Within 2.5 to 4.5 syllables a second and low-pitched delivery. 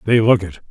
No: 5.9 syllables/s; low, 105 Hz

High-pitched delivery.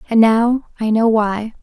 Yes: high, 225 Hz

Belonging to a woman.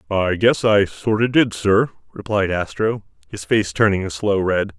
No: male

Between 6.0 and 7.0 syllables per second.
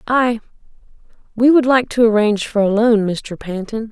No: 5.0 syllables/s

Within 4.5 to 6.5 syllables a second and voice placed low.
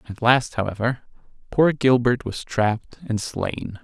No: 4.2 syllables/s; low, 120 Hz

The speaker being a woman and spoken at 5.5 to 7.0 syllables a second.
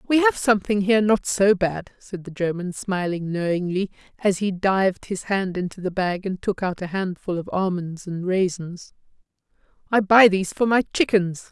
No: female; 4.9 syllables/s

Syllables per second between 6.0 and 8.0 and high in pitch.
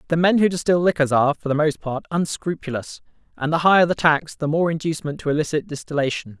No: 6.4 syllables/s; medium, 155 Hz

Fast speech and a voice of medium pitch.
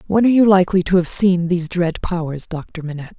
Yes: fast, 225 wpm; medium, 175 Hz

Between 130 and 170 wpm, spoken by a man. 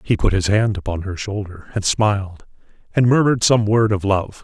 No: fast, 205 wpm; male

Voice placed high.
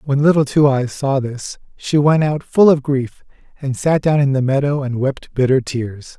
No: low, 135 Hz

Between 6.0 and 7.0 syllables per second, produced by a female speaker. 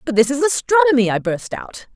No: 5.6 syllables/s; female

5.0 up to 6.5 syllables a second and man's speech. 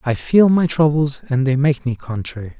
Yes: 5.1 syllables/s; male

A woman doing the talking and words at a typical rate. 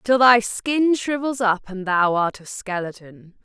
Yes: female; average, 175 wpm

